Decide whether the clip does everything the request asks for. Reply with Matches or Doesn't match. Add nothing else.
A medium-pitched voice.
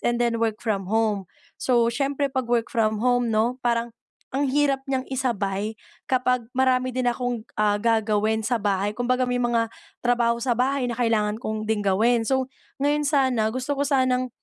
Doesn't match